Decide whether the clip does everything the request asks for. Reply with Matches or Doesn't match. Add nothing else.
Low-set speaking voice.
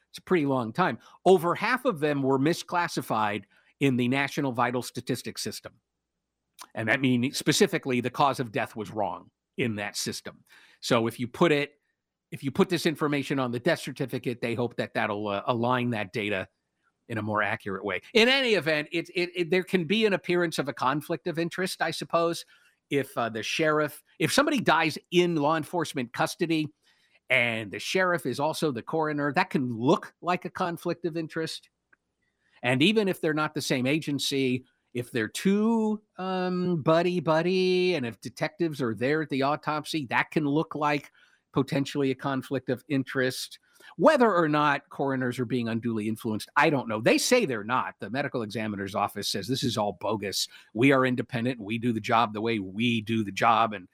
Doesn't match